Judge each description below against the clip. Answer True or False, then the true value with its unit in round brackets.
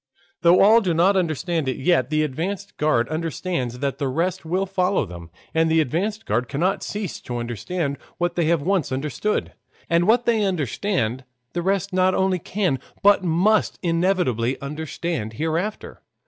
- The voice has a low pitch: False (170 Hz)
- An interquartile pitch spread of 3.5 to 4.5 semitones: False (5.2 semitones)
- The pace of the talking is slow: False (160 wpm)